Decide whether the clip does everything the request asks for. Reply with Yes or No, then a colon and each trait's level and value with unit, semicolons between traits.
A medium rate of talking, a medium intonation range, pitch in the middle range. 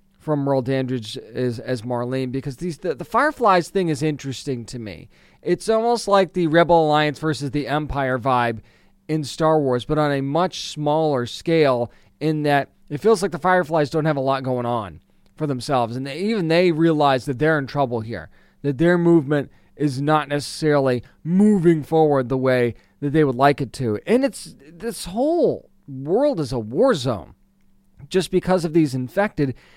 Yes: average, 180 wpm; average, 4.6 semitones; medium, 145 Hz